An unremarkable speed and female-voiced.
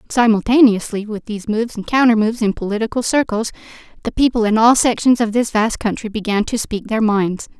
Yes: average, 190 wpm; female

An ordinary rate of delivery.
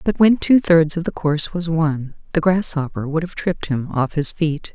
No: fast, 230 wpm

